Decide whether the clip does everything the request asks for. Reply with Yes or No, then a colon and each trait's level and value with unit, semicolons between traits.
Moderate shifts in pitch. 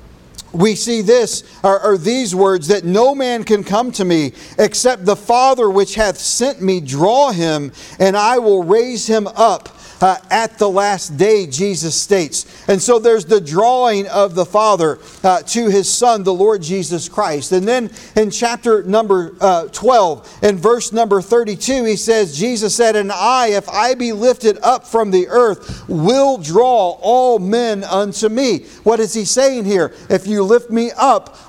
Yes: average, 3.5 semitones